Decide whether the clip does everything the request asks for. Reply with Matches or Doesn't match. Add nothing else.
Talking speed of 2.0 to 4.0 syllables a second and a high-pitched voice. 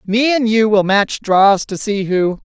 Matches